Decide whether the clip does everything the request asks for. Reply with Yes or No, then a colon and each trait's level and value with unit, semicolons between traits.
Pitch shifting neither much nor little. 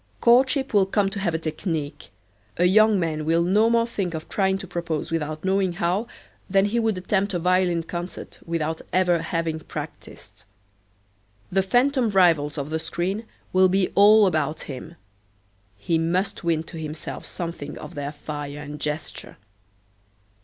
Yes: average, 3.5 semitones